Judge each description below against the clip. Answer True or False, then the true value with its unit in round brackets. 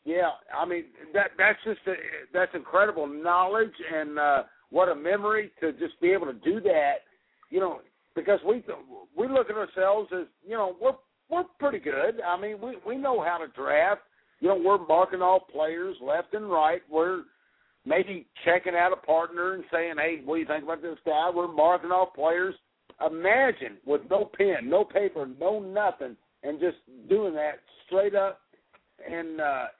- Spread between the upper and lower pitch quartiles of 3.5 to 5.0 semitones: True (4.4 semitones)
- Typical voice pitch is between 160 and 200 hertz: True (185 Hz)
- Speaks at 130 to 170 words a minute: False (180 wpm)